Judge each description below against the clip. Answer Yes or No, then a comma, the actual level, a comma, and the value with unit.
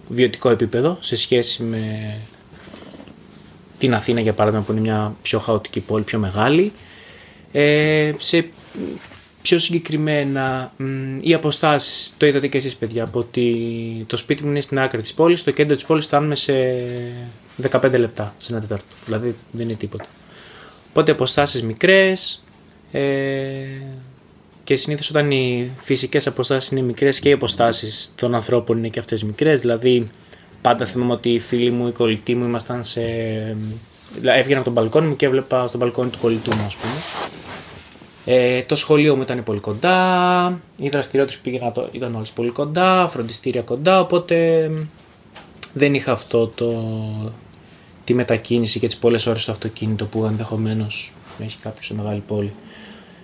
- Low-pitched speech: Yes, low, 125 Hz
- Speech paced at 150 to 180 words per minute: Yes, average, 155 wpm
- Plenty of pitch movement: No, average, 4.1 semitones